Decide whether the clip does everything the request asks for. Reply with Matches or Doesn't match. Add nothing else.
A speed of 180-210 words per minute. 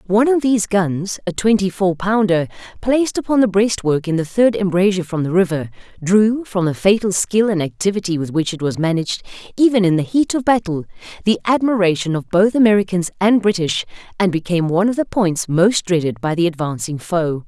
Matches